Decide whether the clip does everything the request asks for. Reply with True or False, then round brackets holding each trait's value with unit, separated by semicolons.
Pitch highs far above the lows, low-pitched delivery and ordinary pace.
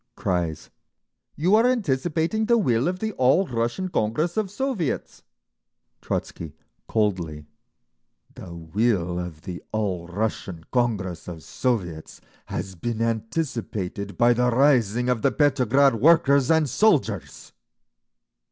False (8.5 semitones; 120 Hz; 115 wpm)